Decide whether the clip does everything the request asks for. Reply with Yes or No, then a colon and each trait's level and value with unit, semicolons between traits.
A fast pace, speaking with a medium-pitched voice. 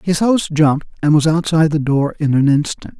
Yes: fast, 220 wpm; medium, 155 Hz